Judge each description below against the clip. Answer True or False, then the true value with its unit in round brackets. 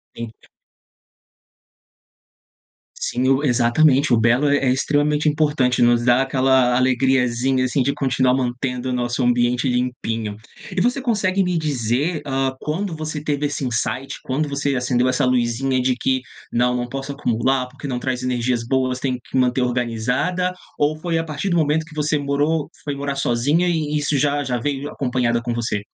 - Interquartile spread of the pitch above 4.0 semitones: False (3.0 semitones)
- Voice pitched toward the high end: False (130 Hz)